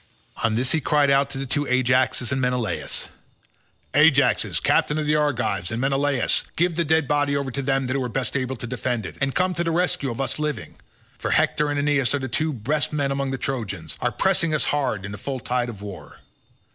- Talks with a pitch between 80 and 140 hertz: Yes, low, 135 Hz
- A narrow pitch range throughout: No, average, 3.0 semitones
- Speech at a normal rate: No, fast, 225 wpm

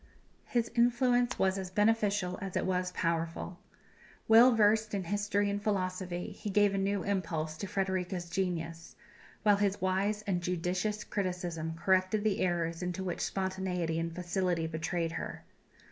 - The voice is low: No, high, 190 Hz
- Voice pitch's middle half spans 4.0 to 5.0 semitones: No, average, 2.7 semitones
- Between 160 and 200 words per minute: No, average, 145 wpm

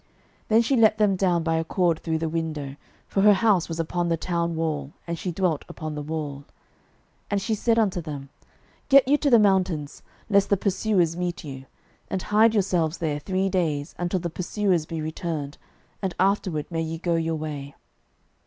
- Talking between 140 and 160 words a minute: No, average, 195 wpm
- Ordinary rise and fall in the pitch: Yes, average, 3.7 semitones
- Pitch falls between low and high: Yes, medium, 170 Hz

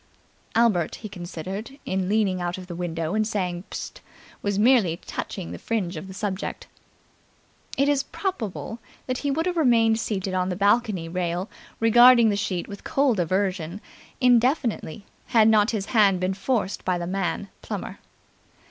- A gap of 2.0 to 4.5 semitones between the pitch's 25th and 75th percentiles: Yes, average, 4.0 semitones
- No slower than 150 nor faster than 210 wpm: Yes, average, 165 wpm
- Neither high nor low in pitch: No, high, 200 Hz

